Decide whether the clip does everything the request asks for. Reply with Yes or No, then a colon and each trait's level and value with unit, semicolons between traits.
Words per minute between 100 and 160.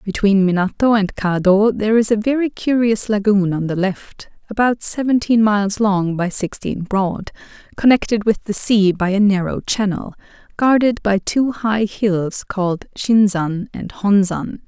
Yes: average, 150 wpm